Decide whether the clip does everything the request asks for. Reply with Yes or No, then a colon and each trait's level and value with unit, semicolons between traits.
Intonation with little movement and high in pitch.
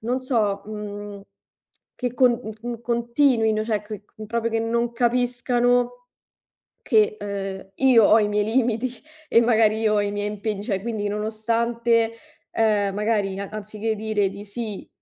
Yes: narrow, 2.2 semitones; high, 220 Hz